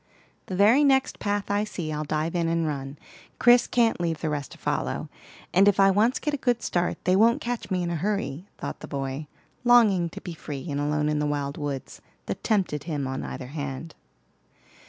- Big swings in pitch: Yes, wide, 5.7 semitones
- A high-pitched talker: No, medium, 170 Hz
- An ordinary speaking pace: No, fast, 210 wpm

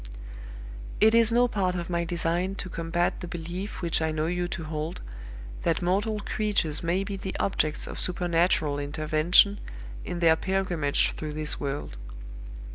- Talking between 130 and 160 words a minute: Yes, average, 155 wpm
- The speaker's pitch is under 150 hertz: No, medium, 175 Hz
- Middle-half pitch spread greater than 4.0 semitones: No, average, 3.2 semitones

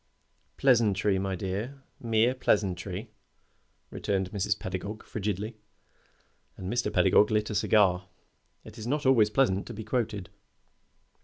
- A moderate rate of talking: No, slow, 125 wpm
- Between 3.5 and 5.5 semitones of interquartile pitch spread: No, average, 2.9 semitones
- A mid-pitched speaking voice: No, low, 105 Hz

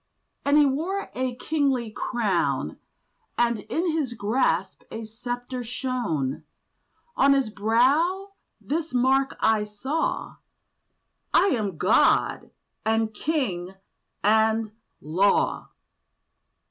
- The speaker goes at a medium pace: No, slow, 95 wpm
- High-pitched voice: Yes, high, 240 Hz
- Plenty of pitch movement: No, average, 4.6 semitones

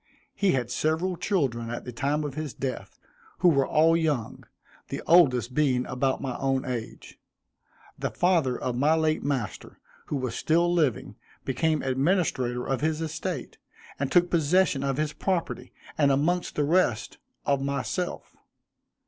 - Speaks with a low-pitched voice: No, medium, 145 Hz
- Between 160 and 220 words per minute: No, average, 150 wpm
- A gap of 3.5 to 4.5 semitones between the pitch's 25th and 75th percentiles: Yes, average, 4.0 semitones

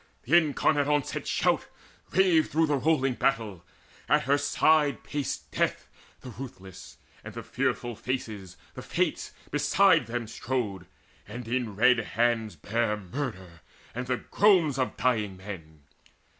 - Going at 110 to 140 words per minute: Yes, slow, 135 wpm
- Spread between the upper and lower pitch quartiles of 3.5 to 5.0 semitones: No, wide, 5.6 semitones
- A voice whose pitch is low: Yes, low, 120 Hz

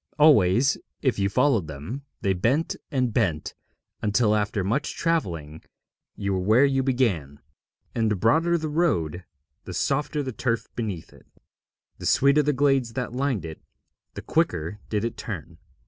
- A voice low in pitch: Yes, low, 115 Hz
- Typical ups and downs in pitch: No, wide, 6.8 semitones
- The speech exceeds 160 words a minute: No, average, 155 wpm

